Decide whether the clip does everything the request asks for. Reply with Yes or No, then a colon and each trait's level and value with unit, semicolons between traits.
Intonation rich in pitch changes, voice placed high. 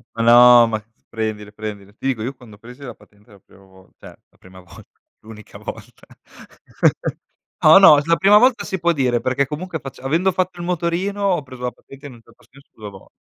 No: wide, 7.4 semitones; low, 125 Hz